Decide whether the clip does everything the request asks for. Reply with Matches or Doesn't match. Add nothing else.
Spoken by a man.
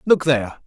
Matches